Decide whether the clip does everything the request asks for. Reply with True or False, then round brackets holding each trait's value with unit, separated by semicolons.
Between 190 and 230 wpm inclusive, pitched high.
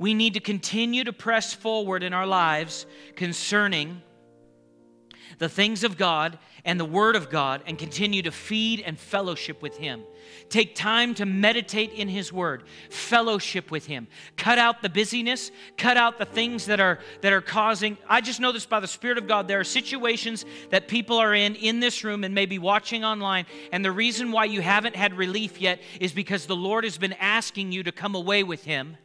True (200 wpm; 200 Hz)